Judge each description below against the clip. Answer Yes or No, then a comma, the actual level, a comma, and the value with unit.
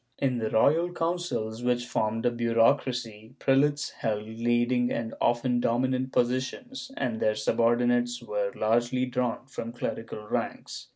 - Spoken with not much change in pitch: Yes, narrow, 2.3 semitones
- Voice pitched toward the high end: No, low, 120 Hz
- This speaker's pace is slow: Yes, slow, 130 wpm